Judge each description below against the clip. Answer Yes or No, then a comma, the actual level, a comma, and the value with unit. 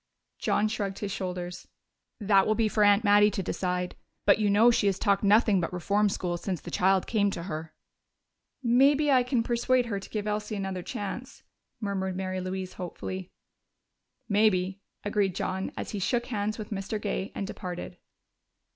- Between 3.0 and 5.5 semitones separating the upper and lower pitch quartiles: No, narrow, 2.4 semitones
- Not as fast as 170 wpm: No, average, 175 wpm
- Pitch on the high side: Yes, high, 200 Hz